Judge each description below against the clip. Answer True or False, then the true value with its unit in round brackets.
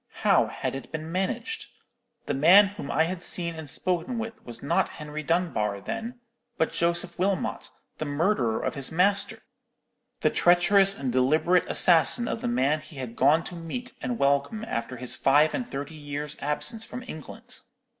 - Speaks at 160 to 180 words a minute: True (165 wpm)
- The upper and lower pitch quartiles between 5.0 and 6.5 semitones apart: True (5.4 semitones)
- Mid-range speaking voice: True (160 Hz)